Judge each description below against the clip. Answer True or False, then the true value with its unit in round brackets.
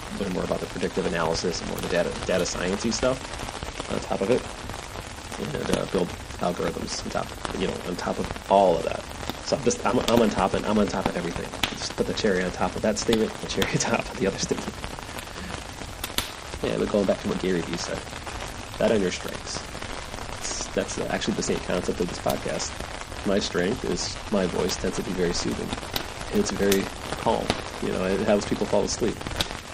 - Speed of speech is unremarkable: False (210 wpm)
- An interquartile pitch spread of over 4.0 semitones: False (3.0 semitones)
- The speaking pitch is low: True (100 Hz)